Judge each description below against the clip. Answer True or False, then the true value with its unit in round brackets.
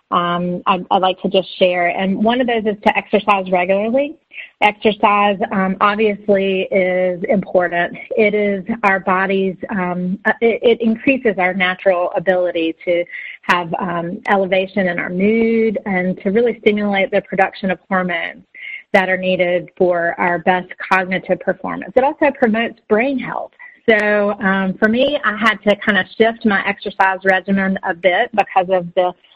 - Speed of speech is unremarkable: True (155 wpm)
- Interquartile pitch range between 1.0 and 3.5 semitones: True (3.0 semitones)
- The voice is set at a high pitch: True (195 Hz)